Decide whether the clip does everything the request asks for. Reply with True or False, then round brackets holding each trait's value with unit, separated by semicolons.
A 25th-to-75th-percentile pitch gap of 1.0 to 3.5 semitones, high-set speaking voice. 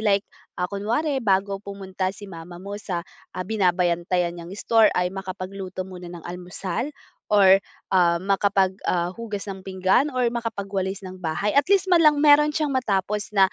True (2.8 semitones; 195 Hz)